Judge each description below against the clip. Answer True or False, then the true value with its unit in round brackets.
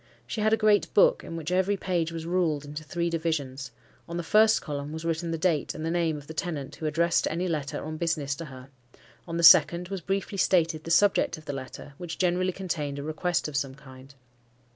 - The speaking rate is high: True (225 wpm)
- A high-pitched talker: False (165 Hz)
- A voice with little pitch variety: False (3.1 semitones)